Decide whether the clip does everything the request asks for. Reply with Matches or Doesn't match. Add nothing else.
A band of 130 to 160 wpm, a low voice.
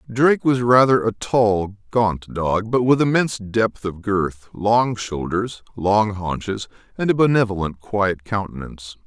Matches